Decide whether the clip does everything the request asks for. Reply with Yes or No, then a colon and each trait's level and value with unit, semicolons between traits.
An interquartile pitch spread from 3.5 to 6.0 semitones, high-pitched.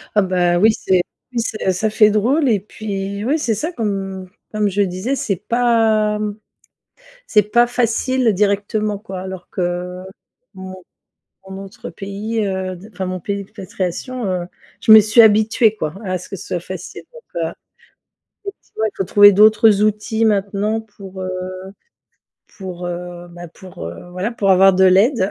No: average, 2.7 semitones; high, 200 Hz